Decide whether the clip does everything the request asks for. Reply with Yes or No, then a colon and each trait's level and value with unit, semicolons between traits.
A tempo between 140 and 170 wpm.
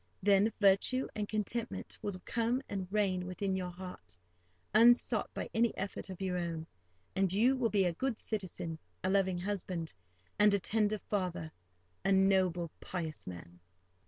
Yes: average, 150 wpm